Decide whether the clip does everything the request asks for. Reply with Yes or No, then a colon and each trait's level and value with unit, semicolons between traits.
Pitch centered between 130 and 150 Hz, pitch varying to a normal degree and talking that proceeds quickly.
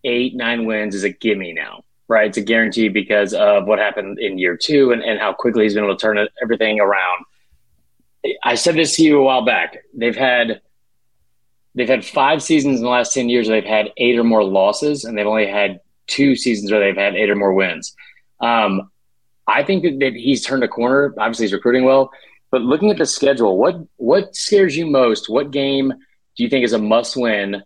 No: low, 120 Hz; average, 4.0 semitones; fast, 215 wpm